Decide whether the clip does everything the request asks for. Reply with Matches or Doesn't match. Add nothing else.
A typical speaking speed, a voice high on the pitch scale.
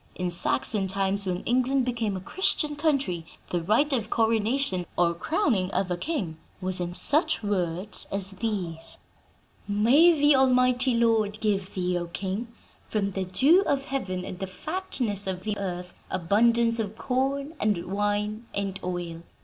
Matches